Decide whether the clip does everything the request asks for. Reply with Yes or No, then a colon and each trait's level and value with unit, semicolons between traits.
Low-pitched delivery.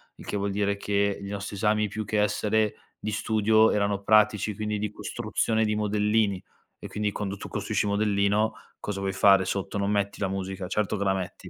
Yes: low, 105 Hz